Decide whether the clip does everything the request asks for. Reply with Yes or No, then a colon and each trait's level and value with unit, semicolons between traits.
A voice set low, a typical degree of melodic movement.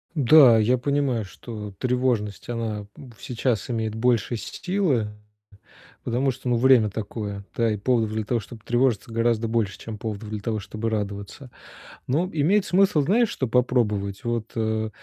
Yes: low, 115 Hz; average, 3.0 semitones